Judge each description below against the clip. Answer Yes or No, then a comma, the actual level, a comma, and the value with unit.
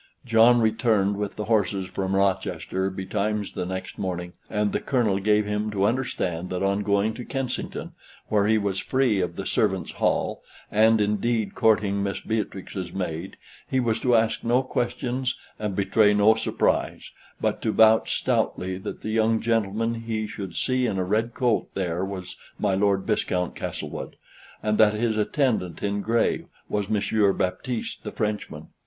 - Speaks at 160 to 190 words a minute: Yes, average, 165 wpm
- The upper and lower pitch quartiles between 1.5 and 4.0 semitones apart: Yes, narrow, 2.5 semitones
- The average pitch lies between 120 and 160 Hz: No, low, 105 Hz